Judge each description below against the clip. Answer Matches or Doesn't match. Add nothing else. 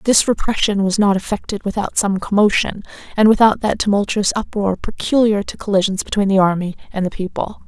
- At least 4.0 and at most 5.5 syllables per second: Doesn't match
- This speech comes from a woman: Matches